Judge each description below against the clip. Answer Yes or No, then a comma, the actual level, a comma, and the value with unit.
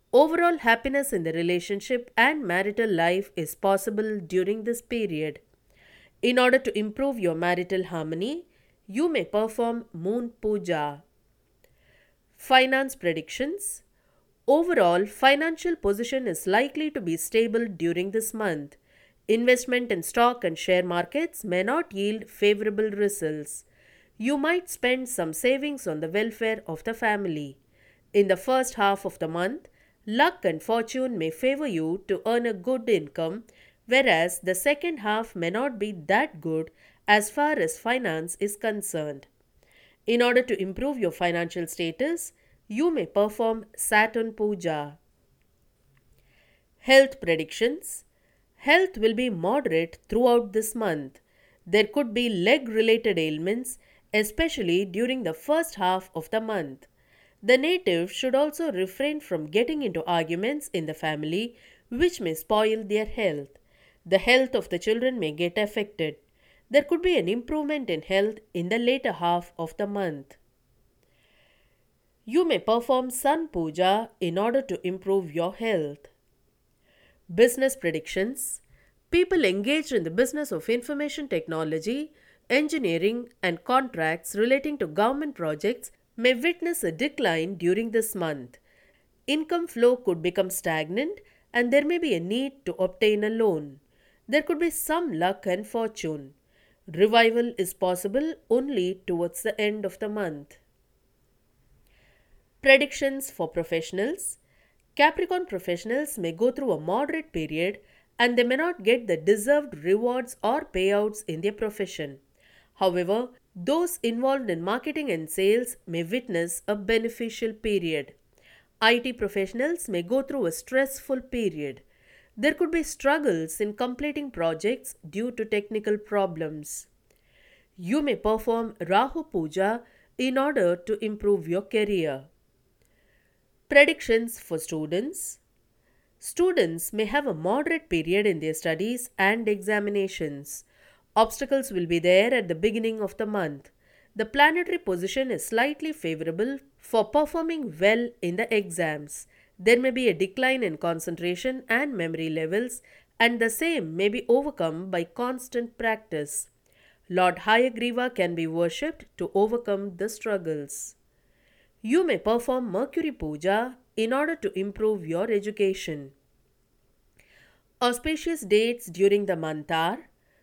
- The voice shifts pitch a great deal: Yes, wide, 6.5 semitones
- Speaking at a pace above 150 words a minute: No, slow, 135 wpm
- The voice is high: Yes, high, 215 Hz